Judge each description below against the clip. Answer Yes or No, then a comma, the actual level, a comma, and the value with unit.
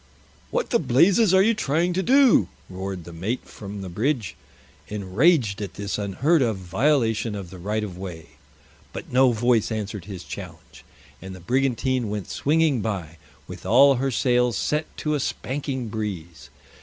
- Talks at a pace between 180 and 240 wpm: No, average, 165 wpm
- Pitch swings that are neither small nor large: No, wide, 6.0 semitones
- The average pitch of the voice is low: Yes, low, 115 Hz